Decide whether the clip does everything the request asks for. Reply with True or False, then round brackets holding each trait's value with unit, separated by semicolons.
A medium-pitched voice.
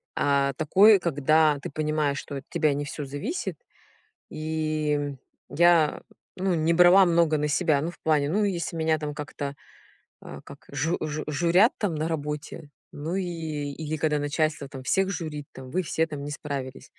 True (155 Hz)